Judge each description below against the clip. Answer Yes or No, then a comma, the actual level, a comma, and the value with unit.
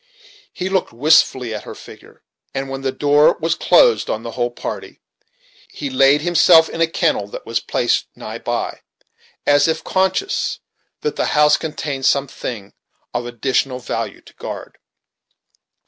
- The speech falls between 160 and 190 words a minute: No, average, 150 wpm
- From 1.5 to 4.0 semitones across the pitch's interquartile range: No, average, 4.4 semitones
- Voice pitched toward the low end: No, medium, 145 Hz